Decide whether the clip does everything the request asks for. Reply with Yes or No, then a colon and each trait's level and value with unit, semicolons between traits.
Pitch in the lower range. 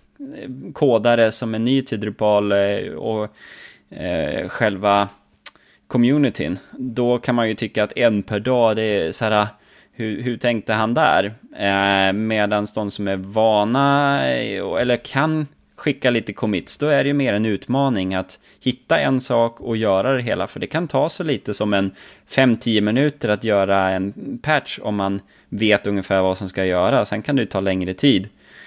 Yes: low, 110 Hz